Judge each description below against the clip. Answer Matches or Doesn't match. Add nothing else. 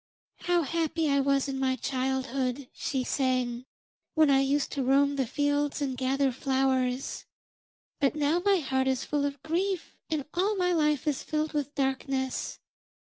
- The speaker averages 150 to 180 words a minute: Matches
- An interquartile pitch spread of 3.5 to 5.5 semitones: Doesn't match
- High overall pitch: Matches